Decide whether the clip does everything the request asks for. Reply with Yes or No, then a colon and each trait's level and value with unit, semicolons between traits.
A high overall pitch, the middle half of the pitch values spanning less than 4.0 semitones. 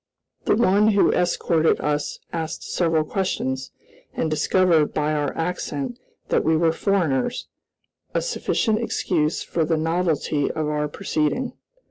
No: medium, 160 Hz; average, 3.6 semitones